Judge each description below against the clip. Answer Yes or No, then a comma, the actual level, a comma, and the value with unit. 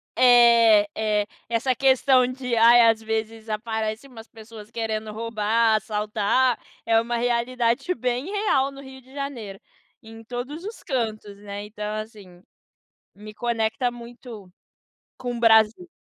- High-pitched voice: Yes, high, 230 Hz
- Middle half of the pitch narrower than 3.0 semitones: Yes, narrow, 2.4 semitones